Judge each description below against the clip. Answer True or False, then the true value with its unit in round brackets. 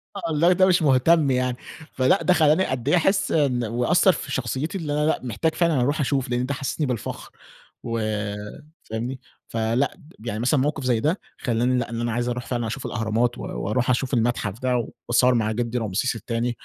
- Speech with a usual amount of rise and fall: True (3.9 semitones)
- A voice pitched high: False (125 Hz)